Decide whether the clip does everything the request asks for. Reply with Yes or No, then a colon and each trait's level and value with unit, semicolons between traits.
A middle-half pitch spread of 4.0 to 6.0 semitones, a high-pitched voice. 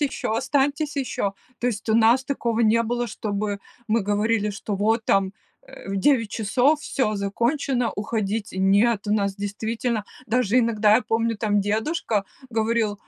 No: average, 2.7 semitones; high, 220 Hz